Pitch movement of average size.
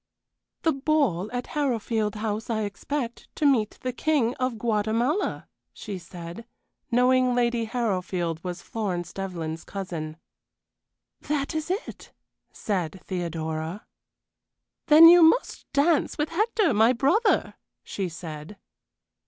No: wide, 7.3 semitones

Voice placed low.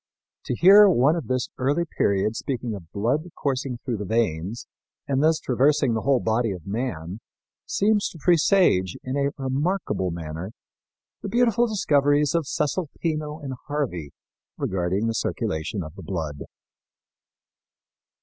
Yes: low, 130 Hz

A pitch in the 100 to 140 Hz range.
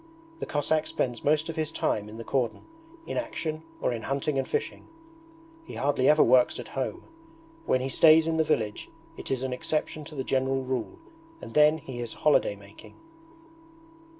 Yes: low, 135 Hz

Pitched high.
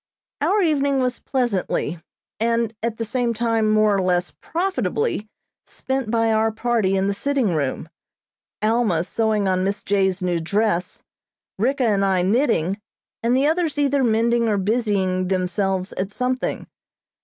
Yes: high, 220 Hz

